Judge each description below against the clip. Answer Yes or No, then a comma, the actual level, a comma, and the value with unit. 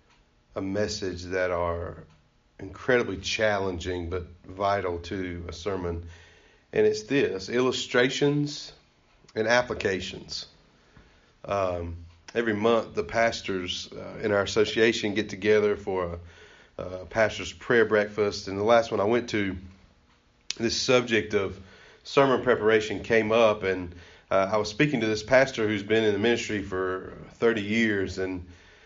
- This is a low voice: Yes, low, 100 Hz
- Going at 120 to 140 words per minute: Yes, slow, 135 wpm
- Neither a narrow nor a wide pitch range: Yes, average, 3.5 semitones